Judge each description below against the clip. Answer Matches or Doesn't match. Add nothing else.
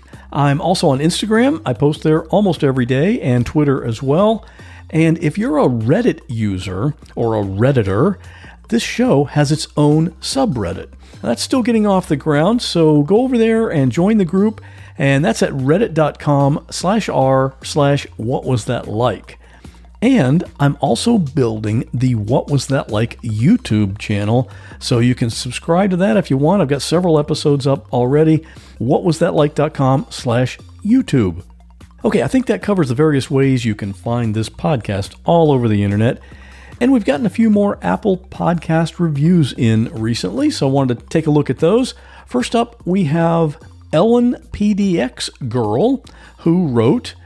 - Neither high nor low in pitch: Matches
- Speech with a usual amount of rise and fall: Doesn't match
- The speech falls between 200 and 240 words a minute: Doesn't match